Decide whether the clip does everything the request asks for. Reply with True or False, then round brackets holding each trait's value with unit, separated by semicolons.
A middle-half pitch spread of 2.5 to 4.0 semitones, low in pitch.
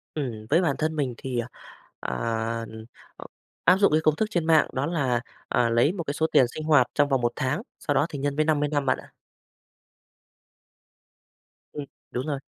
False (3.4 semitones; 145 Hz)